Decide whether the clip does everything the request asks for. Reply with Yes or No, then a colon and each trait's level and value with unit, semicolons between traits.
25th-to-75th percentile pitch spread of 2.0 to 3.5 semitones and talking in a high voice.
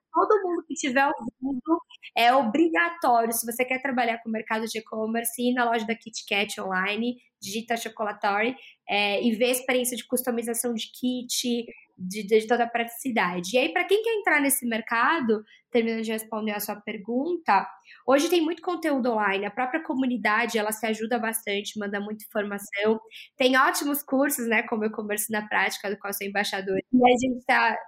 Yes: average, 3.2 semitones; high, 235 Hz